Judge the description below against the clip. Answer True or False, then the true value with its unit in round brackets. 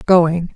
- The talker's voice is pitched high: False (170 Hz)